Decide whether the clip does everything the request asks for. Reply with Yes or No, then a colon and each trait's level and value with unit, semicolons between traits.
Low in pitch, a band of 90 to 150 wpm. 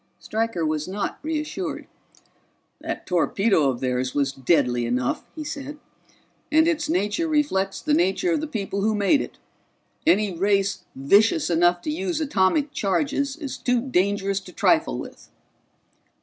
No: high, 205 Hz; average, 145 wpm